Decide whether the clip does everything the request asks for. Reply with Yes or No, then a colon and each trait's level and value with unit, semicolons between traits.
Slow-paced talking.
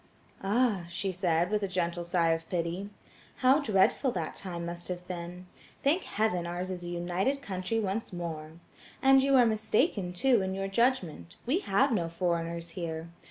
No: average, 170 wpm